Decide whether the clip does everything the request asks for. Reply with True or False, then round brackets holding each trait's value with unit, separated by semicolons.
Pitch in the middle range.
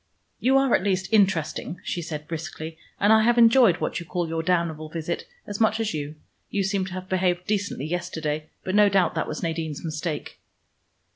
True (180 Hz)